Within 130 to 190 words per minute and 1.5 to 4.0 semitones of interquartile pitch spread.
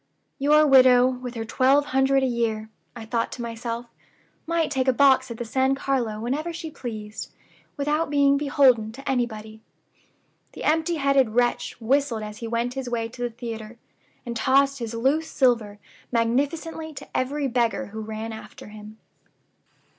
Yes: average, 160 wpm; average, 3.4 semitones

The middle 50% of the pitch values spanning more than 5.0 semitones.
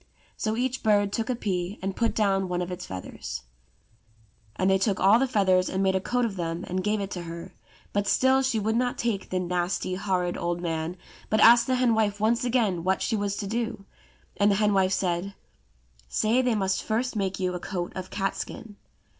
No: average, 3.3 semitones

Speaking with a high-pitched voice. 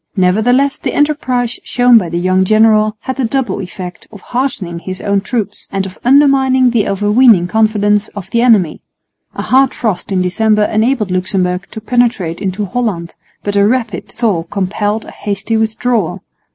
Yes: high, 215 Hz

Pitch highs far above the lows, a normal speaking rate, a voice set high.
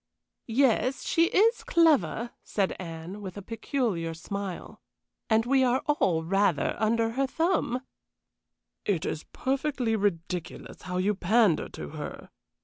No: wide, 6.3 semitones; slow, 130 wpm; high, 220 Hz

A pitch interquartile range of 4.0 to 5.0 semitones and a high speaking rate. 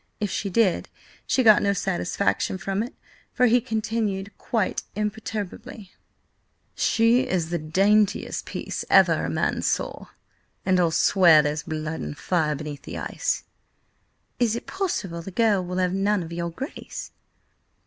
No: average, 4.3 semitones; average, 150 wpm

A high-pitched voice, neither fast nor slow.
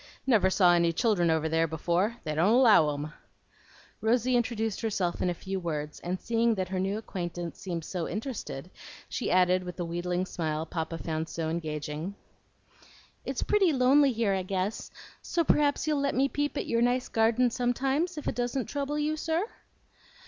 Yes: high, 195 Hz; average, 175 wpm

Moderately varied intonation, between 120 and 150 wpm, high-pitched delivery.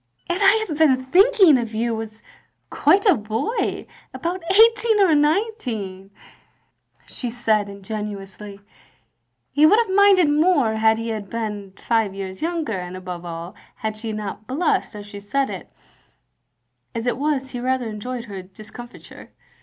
No: wide, 7.5 semitones; average, 145 wpm; high, 230 Hz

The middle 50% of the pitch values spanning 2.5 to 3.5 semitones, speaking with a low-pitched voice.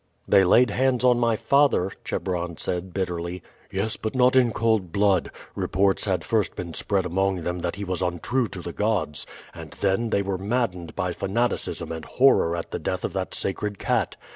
No: average, 4.1 semitones; very low, 95 Hz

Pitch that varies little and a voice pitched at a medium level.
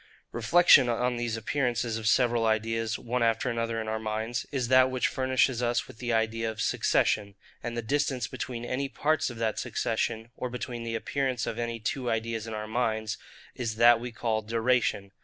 No: narrow, 1.9 semitones; low, 115 Hz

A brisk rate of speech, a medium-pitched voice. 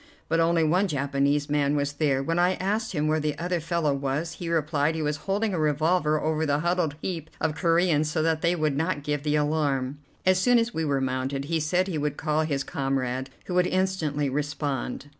Yes: fast, 215 wpm; medium, 155 Hz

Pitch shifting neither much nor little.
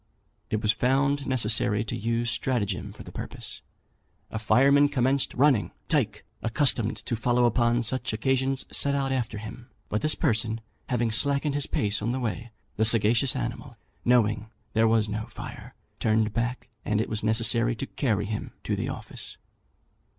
Yes: average, 3.2 semitones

